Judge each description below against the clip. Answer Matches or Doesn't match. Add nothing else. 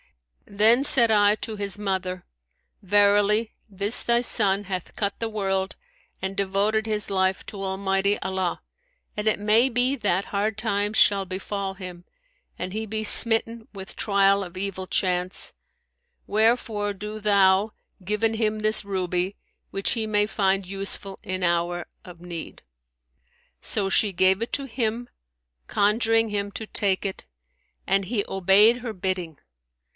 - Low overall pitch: Doesn't match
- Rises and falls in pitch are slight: Matches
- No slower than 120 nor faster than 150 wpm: Matches